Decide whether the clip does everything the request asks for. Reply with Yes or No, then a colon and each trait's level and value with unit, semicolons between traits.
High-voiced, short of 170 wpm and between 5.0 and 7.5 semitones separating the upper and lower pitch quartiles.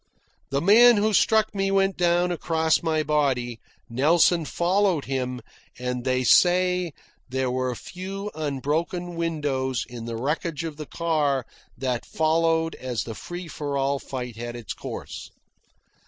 No: medium, 155 Hz; average, 140 wpm; average, 5.3 semitones